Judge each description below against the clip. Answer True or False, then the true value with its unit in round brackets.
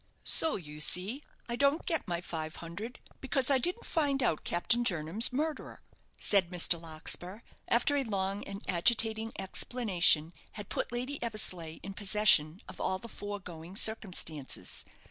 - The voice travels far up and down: True (5.7 semitones)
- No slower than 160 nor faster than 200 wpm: False (145 wpm)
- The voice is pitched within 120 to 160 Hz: False (200 Hz)